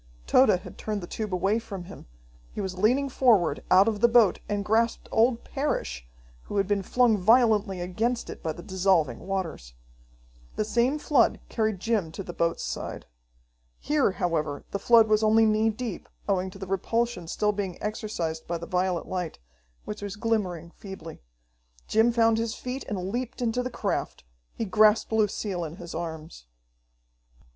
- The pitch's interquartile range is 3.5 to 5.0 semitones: Yes, average, 4.1 semitones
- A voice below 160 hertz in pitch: No, high, 205 Hz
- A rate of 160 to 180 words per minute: Yes, average, 170 wpm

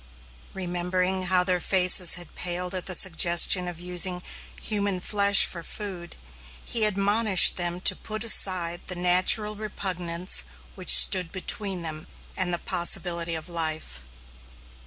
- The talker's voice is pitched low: No, medium, 180 Hz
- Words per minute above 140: No, slow, 135 wpm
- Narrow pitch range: Yes, narrow, 1.9 semitones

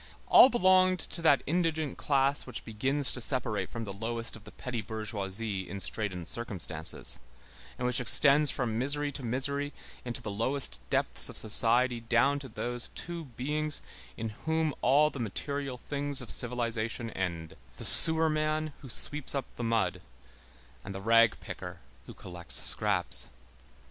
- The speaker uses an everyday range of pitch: Yes, average, 4.5 semitones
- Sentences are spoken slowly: No, average, 155 wpm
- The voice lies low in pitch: Yes, low, 125 Hz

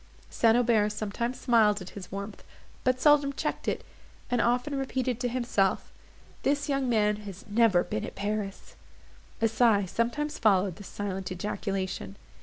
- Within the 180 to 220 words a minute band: No, average, 150 wpm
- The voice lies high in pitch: Yes, high, 215 Hz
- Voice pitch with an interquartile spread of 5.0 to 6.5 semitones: No, average, 3.7 semitones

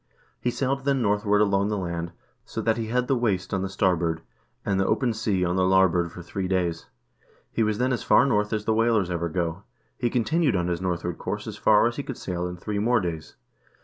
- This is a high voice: No, low, 100 Hz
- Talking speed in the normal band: No, fast, 240 wpm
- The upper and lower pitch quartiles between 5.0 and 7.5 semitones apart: No, average, 4.4 semitones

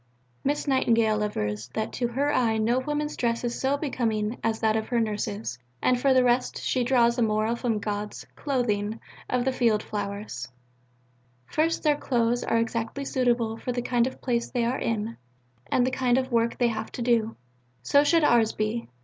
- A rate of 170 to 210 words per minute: Yes, average, 190 wpm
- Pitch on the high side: Yes, high, 235 Hz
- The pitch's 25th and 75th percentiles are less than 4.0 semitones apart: Yes, narrow, 2.6 semitones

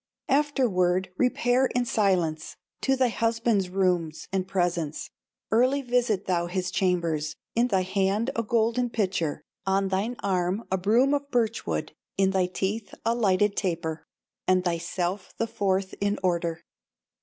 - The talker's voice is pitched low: No, high, 195 Hz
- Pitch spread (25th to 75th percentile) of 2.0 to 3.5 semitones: No, average, 4.3 semitones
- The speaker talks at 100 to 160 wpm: Yes, average, 145 wpm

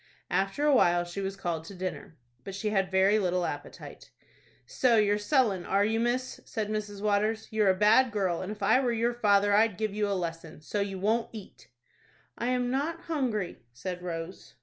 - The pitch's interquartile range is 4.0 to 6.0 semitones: No, average, 3.2 semitones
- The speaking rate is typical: Yes, average, 195 wpm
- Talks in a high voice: Yes, high, 205 Hz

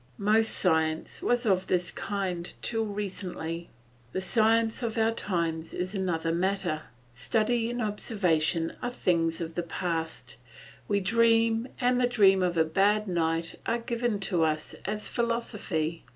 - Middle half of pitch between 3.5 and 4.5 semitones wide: No, average, 5.1 semitones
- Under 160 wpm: Yes, average, 145 wpm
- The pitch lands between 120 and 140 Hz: No, high, 195 Hz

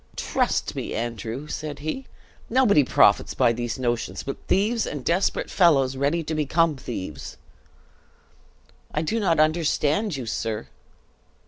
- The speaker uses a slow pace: Yes, slow, 130 wpm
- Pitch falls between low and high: Yes, medium, 150 Hz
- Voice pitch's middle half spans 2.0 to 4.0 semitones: No, average, 5.3 semitones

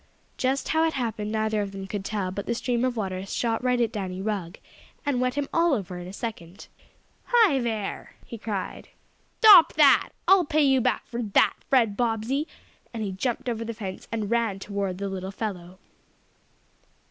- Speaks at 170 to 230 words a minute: Yes, average, 185 wpm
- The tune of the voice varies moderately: Yes, average, 4.4 semitones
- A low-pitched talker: No, high, 225 Hz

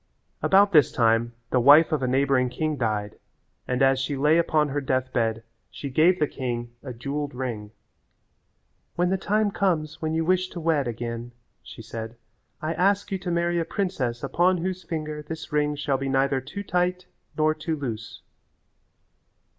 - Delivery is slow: No, average, 175 wpm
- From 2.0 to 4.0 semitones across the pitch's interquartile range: No, average, 5.0 semitones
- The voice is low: No, medium, 150 Hz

